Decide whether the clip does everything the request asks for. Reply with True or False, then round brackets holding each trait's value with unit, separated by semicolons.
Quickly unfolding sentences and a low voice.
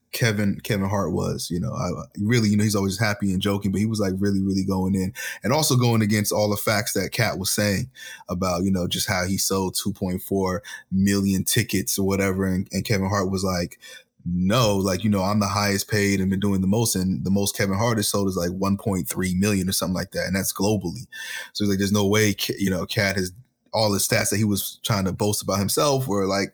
True (240 wpm; 100 Hz)